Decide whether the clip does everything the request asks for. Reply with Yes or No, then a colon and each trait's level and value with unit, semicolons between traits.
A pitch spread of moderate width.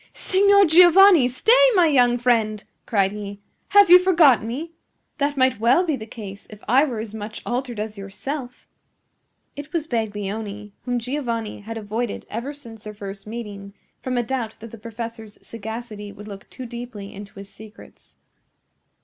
Yes: average, 4.1 semitones